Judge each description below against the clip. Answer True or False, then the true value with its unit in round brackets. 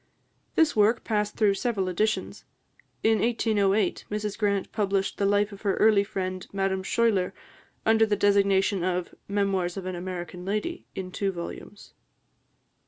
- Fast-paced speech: False (145 wpm)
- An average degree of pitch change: False (2.0 semitones)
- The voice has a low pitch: False (200 Hz)